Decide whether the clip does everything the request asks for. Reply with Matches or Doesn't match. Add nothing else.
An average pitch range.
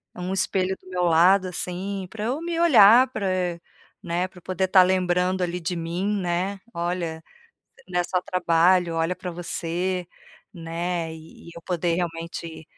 Doesn't match